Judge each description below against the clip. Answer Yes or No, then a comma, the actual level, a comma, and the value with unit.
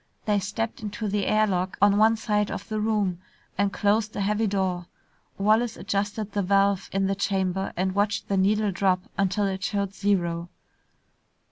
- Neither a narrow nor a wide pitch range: No, narrow, 1.7 semitones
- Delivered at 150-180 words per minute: Yes, average, 170 wpm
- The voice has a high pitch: Yes, high, 200 Hz